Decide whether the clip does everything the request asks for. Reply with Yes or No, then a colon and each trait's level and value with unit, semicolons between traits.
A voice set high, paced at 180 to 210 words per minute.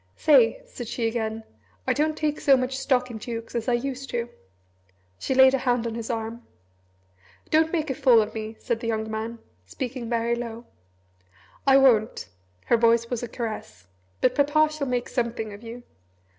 Yes: high, 240 Hz; average, 185 wpm